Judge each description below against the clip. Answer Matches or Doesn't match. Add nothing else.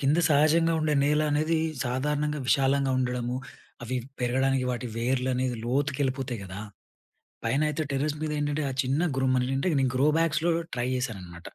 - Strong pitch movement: Doesn't match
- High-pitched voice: Doesn't match